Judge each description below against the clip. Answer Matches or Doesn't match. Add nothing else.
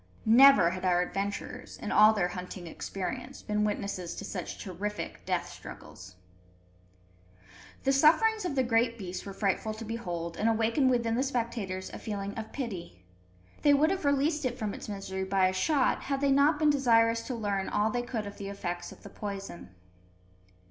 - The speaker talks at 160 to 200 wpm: Matches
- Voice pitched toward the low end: Doesn't match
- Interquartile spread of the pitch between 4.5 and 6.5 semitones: Matches